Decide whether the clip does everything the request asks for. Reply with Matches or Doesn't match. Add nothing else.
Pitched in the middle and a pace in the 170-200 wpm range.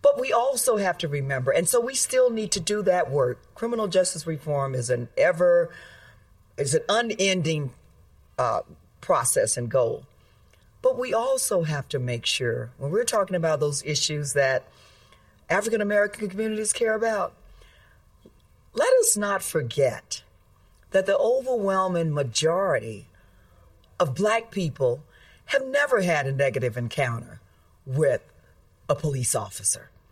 Doesn't match